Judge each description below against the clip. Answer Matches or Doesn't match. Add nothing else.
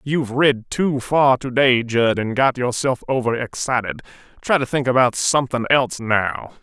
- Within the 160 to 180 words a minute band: Matches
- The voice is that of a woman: Doesn't match